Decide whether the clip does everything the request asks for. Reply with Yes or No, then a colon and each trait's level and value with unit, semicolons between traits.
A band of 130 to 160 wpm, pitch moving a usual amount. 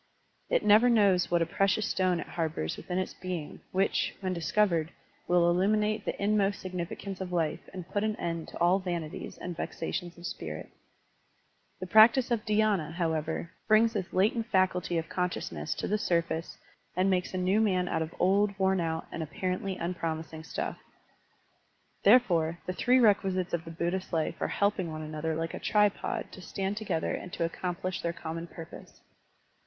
No: average, 175 wpm; average, 3.2 semitones